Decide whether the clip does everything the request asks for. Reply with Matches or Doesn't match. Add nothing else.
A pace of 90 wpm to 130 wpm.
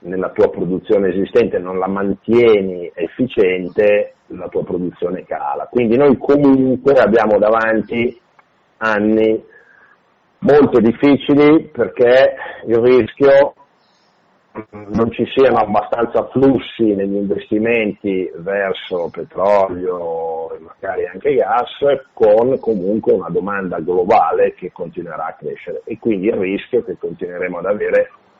Matches